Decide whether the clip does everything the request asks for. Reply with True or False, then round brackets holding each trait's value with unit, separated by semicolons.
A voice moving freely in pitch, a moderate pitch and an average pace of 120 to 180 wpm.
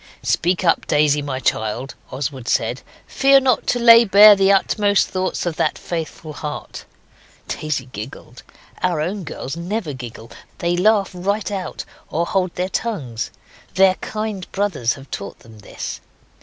True (6.5 semitones; 175 Hz; 150 wpm)